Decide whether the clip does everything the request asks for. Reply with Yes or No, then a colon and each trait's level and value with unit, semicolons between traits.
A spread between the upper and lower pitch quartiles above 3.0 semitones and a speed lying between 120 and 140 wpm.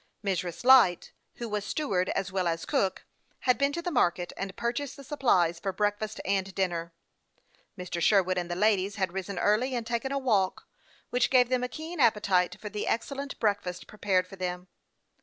No: average, 5.1 semitones; average, 190 wpm